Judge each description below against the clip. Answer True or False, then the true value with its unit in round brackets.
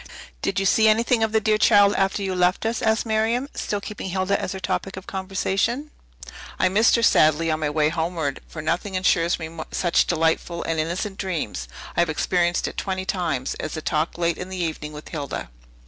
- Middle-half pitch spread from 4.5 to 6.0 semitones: False (3.9 semitones)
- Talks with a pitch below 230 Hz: True (185 Hz)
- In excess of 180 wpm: True (205 wpm)